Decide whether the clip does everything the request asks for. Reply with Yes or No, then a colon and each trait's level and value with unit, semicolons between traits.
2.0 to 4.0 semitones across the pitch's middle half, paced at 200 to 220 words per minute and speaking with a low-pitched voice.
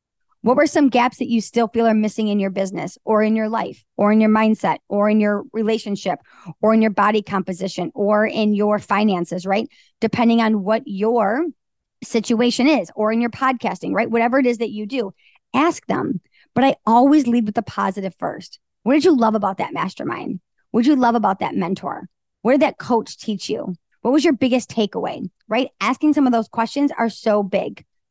No: average, 3.0 semitones; fast, 205 wpm; high, 225 Hz